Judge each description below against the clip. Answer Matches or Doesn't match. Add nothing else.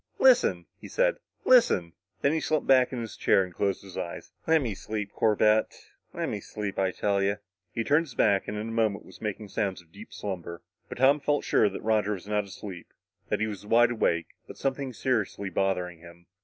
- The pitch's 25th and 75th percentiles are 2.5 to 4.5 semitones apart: Matches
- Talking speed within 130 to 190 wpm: Doesn't match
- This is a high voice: Doesn't match